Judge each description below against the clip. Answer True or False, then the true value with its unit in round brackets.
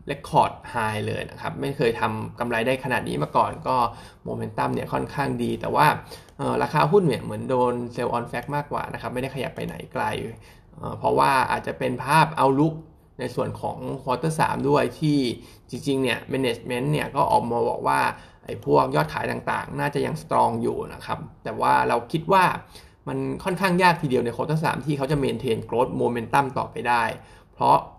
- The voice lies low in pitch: True (130 Hz)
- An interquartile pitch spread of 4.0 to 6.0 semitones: False (3.6 semitones)